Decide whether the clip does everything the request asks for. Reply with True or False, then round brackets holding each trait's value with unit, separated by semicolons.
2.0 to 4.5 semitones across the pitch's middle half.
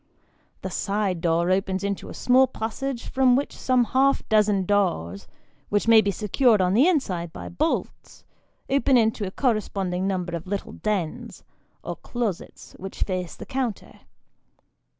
False (5.1 semitones)